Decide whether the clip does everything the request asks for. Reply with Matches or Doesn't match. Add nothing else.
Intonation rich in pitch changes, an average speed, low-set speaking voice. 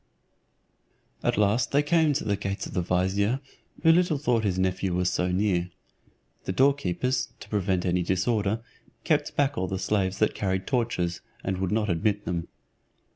Doesn't match